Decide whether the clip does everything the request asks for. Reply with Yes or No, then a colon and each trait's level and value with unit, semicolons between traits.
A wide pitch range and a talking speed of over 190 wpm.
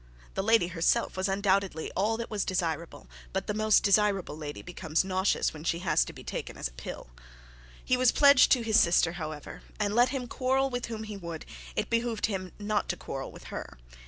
No: average, 4.8 semitones; fast, 205 wpm